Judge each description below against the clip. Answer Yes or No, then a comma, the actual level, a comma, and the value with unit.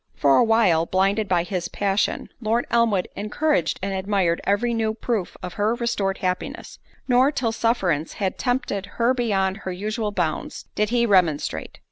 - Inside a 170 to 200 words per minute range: No, average, 160 wpm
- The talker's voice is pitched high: Yes, high, 205 Hz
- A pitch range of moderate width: Yes, average, 3.8 semitones